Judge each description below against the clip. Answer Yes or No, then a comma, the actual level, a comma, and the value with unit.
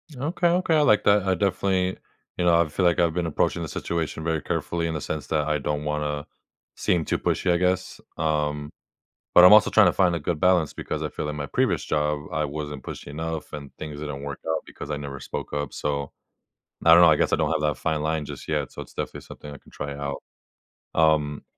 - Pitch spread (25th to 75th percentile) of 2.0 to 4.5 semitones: Yes, average, 2.9 semitones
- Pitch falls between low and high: No, very low, 80 Hz